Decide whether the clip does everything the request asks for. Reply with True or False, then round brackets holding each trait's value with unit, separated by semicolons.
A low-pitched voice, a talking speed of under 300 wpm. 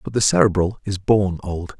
True (95 Hz; 200 wpm)